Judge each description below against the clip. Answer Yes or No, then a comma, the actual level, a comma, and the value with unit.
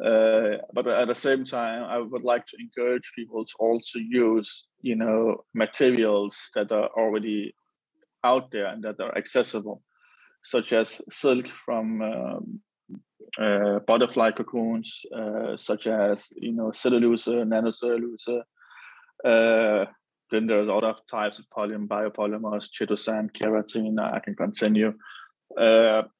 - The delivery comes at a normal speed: No, slow, 130 wpm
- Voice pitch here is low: Yes, low, 115 Hz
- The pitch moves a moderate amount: No, narrow, 1.8 semitones